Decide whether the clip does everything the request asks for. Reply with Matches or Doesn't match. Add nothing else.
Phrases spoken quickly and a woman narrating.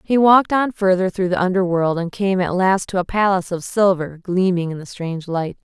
Matches